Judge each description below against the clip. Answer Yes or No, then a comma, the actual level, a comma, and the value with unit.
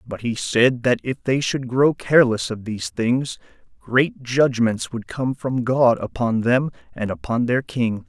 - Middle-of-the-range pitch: No, low, 120 Hz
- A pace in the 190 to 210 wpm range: No, average, 180 wpm